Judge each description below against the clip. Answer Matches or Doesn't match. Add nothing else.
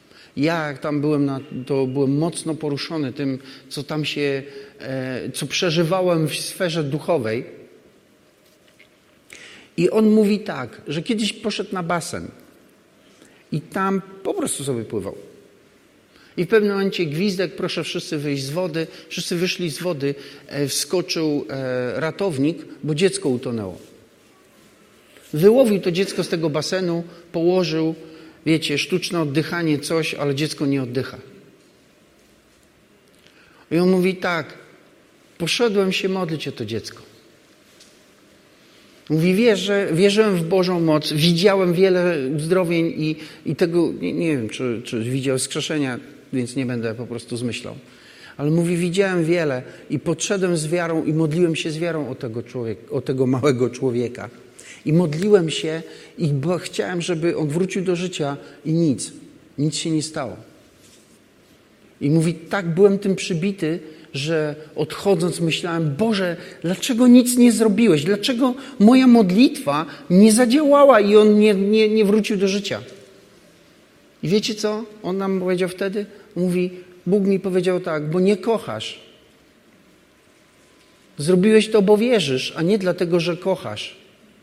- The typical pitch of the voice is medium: Matches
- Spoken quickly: Doesn't match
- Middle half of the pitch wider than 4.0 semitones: Matches